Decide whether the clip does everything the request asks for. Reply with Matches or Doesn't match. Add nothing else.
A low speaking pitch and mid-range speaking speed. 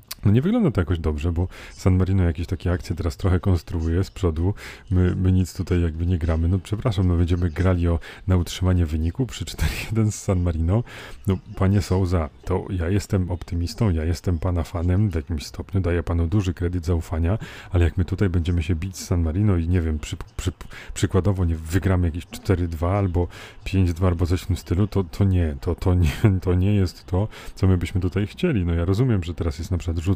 Doesn't match